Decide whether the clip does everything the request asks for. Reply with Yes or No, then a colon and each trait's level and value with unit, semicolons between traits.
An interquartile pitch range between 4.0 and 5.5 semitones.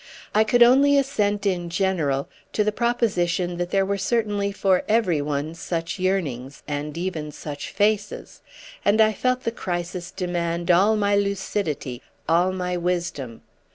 No: average, 3.5 semitones